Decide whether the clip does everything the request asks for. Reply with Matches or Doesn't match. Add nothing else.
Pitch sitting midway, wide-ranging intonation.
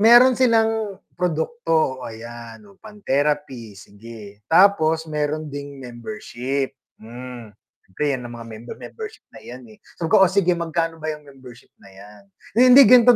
Matches